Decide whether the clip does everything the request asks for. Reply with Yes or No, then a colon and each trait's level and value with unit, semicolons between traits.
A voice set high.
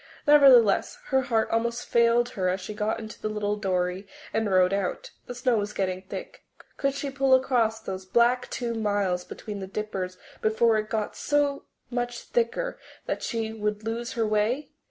Yes: high, 220 Hz